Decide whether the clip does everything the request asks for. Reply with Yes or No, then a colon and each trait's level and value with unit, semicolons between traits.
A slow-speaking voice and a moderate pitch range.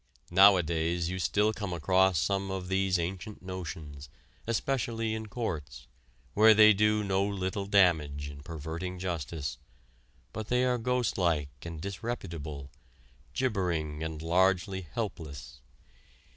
Yes: slow, 120 wpm; average, 4.2 semitones